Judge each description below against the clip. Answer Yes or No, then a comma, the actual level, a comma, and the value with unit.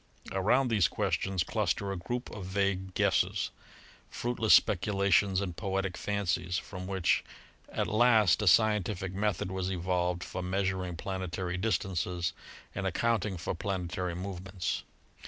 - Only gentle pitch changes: Yes, narrow, 2.0 semitones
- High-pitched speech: No, very low, 95 Hz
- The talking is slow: Yes, slow, 130 wpm